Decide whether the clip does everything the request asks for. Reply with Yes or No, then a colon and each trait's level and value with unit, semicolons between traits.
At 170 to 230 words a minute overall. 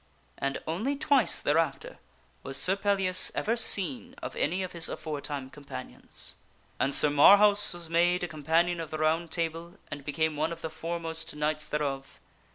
Yes: average, 175 wpm